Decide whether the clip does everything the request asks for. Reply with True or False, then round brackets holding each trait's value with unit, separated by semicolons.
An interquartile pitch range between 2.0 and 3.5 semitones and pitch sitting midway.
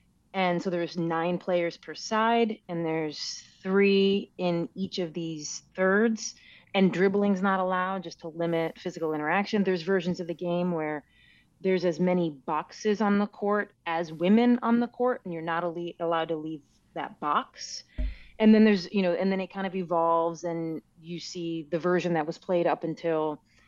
True (2.8 semitones; 175 Hz)